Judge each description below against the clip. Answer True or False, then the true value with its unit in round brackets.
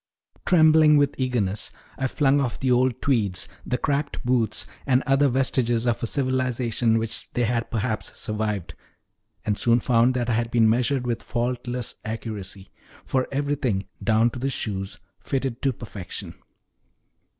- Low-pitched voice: True (120 Hz)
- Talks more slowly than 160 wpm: True (150 wpm)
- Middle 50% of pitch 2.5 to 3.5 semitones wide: True (2.9 semitones)